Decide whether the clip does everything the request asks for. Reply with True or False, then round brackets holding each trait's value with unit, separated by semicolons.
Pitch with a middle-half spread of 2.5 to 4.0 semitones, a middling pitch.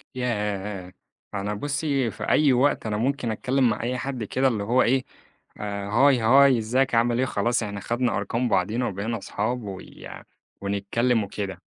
False (3.7 semitones; 115 Hz)